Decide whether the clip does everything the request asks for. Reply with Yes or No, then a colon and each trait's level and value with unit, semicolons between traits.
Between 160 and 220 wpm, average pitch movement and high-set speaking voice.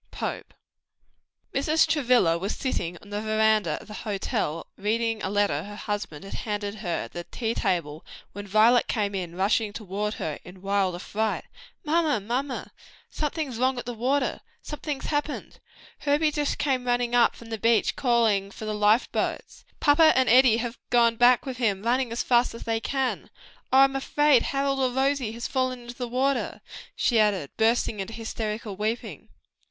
Yes: average, 170 wpm; average, 3.9 semitones; high, 230 Hz